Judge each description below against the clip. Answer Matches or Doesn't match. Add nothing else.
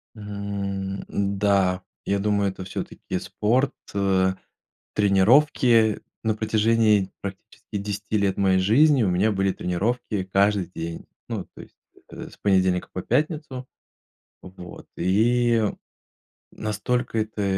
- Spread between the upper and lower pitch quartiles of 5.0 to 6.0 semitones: Doesn't match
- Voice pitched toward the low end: Matches